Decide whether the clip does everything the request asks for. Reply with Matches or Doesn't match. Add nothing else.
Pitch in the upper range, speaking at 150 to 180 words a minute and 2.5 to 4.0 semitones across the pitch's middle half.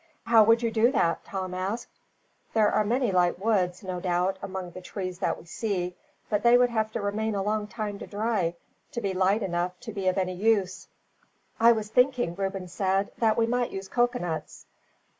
Doesn't match